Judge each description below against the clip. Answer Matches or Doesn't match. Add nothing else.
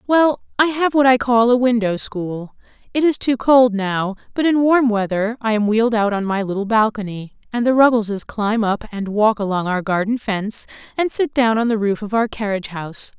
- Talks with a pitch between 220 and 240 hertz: Matches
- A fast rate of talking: Matches